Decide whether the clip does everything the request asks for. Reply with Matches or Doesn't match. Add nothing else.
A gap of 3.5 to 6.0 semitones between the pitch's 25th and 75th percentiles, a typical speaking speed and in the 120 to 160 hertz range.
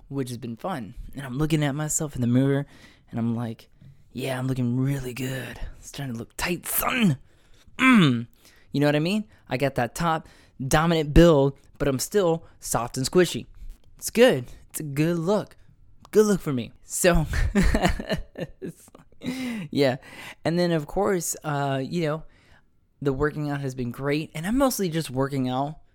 Matches